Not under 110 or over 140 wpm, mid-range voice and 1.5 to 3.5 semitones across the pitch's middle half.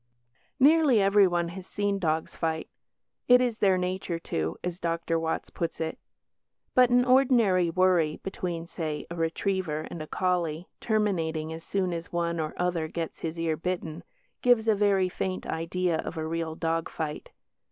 No: average, 165 wpm; medium, 175 Hz; average, 3.1 semitones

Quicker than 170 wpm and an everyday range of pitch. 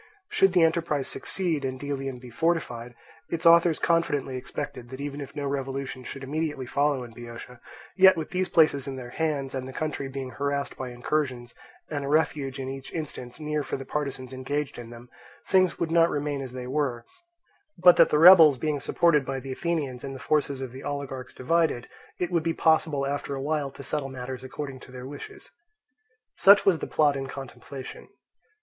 Yes: average, 195 wpm; average, 3.1 semitones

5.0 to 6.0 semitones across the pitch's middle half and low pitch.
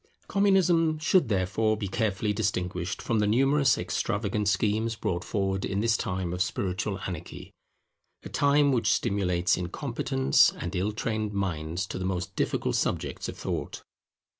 No: average, 3.8 semitones; low, 100 Hz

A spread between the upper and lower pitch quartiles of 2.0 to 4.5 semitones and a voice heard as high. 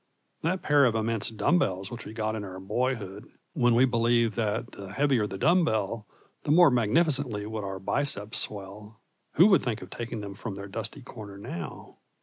No: average, 3.8 semitones; low, 110 Hz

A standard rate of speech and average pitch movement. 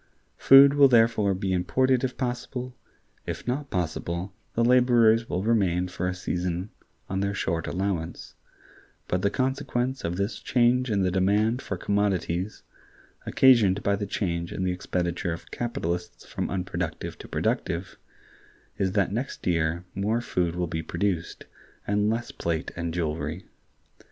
Yes: average, 145 wpm; average, 5.0 semitones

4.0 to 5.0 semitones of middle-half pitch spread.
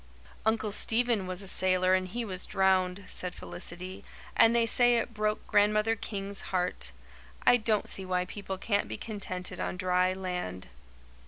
No: average, 2.7 semitones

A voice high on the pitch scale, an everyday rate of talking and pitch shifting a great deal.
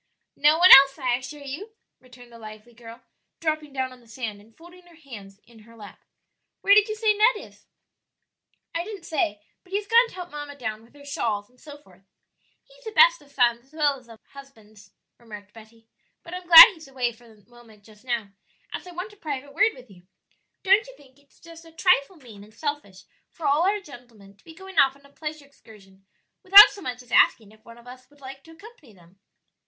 No: very high, 270 Hz; fast, 225 wpm; wide, 6.6 semitones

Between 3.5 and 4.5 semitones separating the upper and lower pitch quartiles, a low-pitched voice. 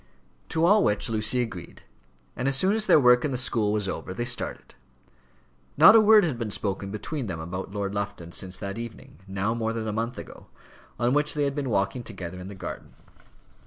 No: average, 5.3 semitones; low, 115 Hz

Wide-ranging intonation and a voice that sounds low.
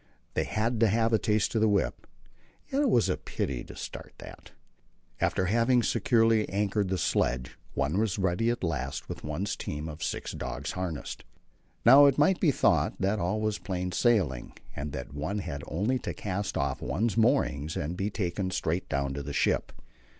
Yes: wide, 6.9 semitones; very low, 95 Hz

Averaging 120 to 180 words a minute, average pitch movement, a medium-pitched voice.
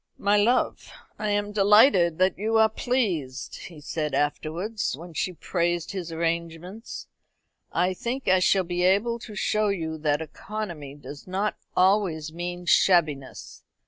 Yes: average, 145 wpm; average, 4.3 semitones; medium, 180 Hz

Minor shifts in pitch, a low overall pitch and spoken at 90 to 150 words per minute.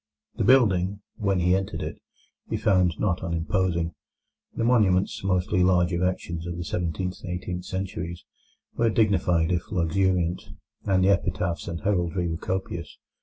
Yes: narrow, 1.9 semitones; very low, 90 Hz; average, 145 wpm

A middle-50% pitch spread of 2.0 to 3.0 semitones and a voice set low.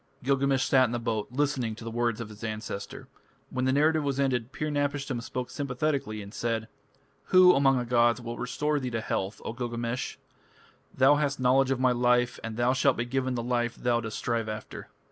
Yes: narrow, 2.6 semitones; low, 125 Hz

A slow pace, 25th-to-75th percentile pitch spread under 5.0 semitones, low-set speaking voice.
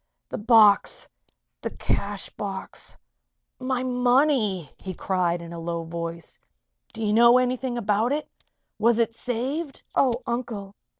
No: slow, 130 wpm; average, 4.6 semitones; high, 225 Hz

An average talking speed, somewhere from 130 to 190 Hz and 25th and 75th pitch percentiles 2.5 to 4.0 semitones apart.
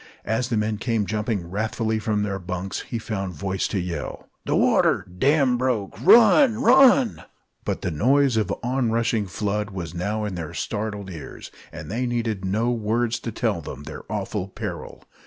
No: average, 175 wpm; low, 110 Hz; average, 3.7 semitones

